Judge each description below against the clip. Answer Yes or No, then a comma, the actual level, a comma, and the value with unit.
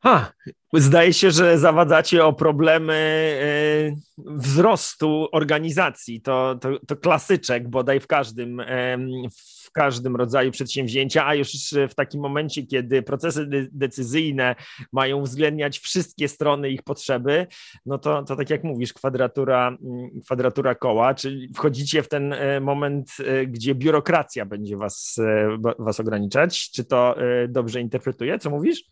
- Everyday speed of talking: Yes, average, 125 wpm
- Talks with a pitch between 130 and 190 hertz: Yes, medium, 140 Hz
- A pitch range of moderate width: Yes, average, 3.1 semitones